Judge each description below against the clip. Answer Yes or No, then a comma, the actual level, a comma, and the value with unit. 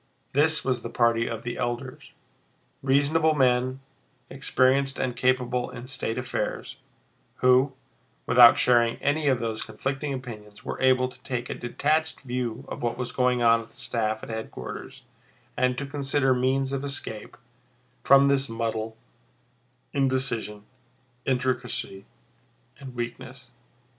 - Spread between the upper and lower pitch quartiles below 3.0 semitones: Yes, narrow, 2.4 semitones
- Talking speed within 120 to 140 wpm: Yes, slow, 135 wpm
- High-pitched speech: No, low, 125 Hz